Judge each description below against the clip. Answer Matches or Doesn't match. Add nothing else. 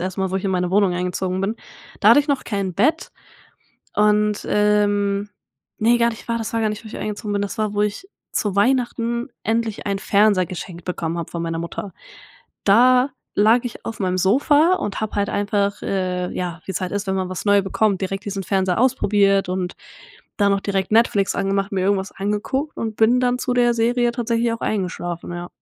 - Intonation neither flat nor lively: Matches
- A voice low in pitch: Doesn't match